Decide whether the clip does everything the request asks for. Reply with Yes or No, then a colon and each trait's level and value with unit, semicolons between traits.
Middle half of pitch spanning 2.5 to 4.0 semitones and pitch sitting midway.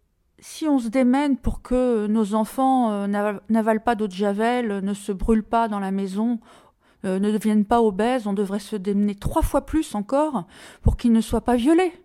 No: average, 3.3 semitones; high, 225 Hz